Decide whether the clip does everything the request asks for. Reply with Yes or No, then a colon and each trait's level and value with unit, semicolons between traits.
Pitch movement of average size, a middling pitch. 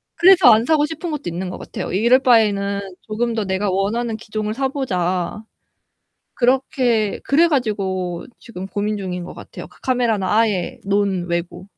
No: average, 4.6 semitones; high, 215 Hz